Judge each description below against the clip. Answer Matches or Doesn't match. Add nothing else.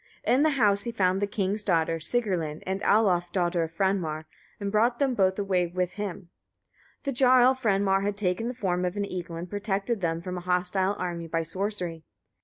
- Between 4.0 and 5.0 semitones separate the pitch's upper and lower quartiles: Doesn't match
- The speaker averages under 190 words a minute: Doesn't match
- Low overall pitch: Doesn't match